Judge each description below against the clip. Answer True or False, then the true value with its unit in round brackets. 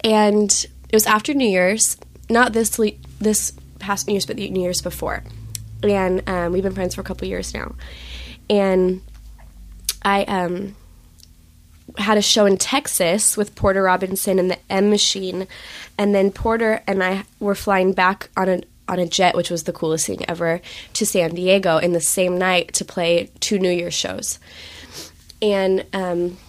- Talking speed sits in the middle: True (175 wpm)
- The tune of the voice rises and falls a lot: False (2.8 semitones)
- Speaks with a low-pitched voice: False (185 Hz)